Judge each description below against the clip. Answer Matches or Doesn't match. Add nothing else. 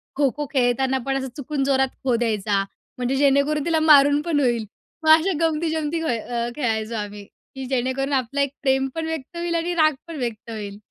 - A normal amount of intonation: Matches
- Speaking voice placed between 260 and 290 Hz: Matches